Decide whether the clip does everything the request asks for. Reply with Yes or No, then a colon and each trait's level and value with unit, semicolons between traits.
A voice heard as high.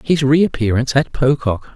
No: low, 135 Hz